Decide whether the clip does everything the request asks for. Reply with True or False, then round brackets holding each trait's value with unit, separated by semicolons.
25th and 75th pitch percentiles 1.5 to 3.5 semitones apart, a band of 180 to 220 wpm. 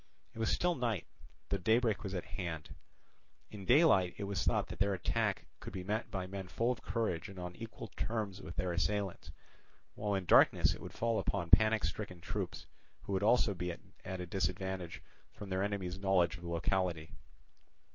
True (3.0 semitones; 185 wpm)